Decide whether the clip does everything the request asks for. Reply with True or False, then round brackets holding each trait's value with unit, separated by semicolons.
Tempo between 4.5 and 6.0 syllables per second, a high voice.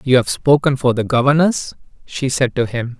False (5.0 syllables/s; 130 Hz)